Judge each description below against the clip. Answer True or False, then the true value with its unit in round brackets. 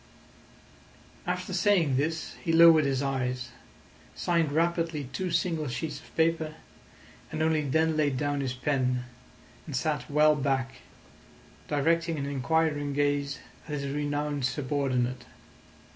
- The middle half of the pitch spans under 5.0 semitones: True (2.8 semitones)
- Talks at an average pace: False (125 wpm)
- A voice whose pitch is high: False (145 Hz)